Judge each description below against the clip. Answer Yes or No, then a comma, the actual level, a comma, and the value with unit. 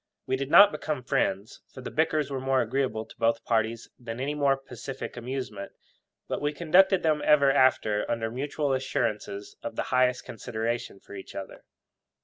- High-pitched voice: No, low, 130 Hz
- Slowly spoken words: No, average, 170 wpm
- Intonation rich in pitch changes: No, average, 3.9 semitones